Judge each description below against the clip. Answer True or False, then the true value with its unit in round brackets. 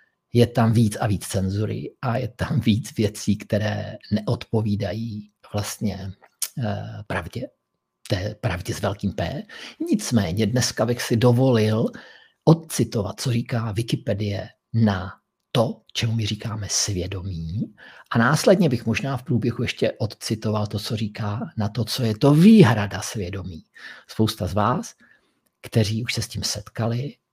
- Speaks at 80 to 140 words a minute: True (135 wpm)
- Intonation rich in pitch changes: False (2.9 semitones)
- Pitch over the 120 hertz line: False (110 Hz)